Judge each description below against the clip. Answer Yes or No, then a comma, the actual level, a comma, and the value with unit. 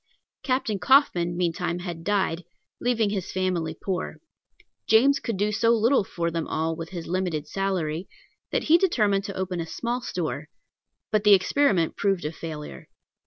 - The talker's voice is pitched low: No, medium, 185 Hz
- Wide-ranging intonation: No, average, 4.2 semitones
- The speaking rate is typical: Yes, average, 160 wpm